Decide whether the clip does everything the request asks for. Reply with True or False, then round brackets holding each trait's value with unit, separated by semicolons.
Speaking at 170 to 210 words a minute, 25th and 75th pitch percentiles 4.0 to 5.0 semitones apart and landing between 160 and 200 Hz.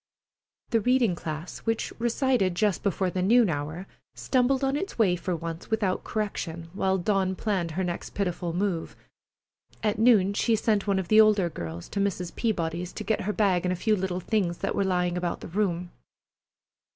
False (185 wpm; 3.6 semitones; 190 Hz)